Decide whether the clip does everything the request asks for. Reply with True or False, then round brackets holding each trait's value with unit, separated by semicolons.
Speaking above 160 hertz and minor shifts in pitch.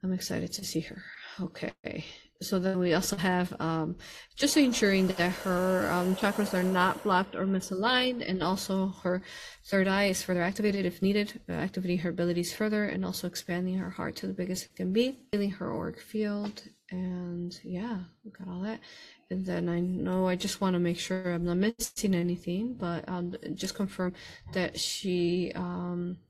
True (185 Hz; 2.0 semitones)